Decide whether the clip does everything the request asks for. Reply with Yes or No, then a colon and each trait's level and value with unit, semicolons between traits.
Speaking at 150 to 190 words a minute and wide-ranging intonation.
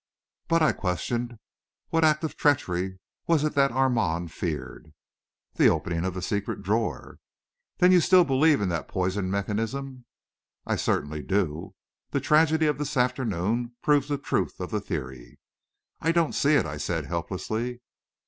Yes: average, 155 wpm; wide, 8.5 semitones